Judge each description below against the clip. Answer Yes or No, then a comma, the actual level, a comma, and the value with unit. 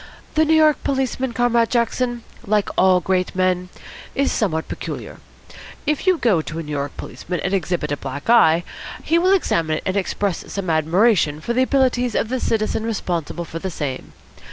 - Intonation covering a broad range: Yes, wide, 6.7 semitones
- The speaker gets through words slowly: No, average, 180 wpm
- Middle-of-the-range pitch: No, high, 200 Hz